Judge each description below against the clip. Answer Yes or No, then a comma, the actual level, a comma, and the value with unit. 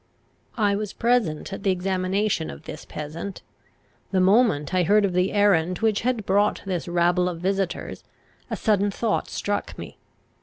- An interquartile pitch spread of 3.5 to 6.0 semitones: No, narrow, 2.5 semitones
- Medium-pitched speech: No, high, 195 Hz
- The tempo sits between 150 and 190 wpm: Yes, average, 160 wpm